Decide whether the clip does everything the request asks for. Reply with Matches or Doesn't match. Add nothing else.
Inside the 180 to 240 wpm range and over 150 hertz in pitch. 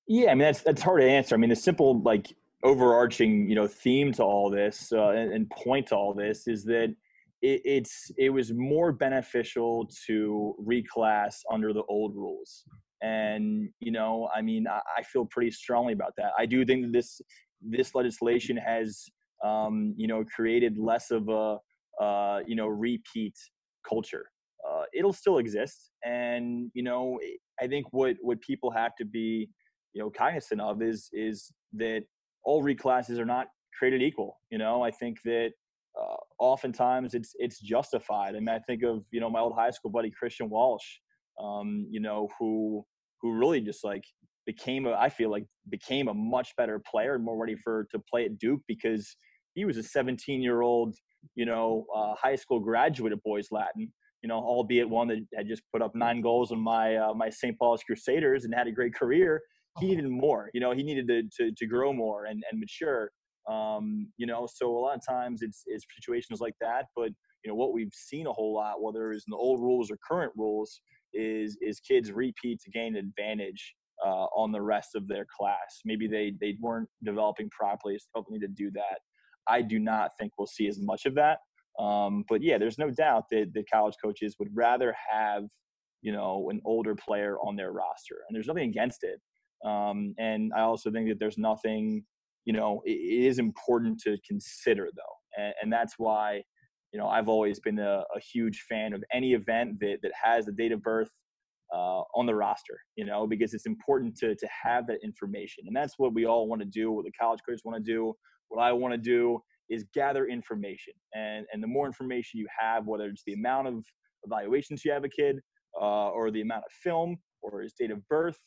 Doesn't match